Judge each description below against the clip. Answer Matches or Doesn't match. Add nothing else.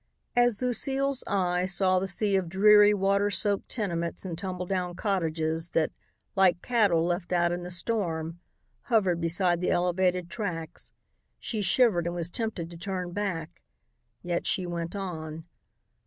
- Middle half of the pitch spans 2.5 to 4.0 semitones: Matches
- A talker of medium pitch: Matches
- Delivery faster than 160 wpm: Doesn't match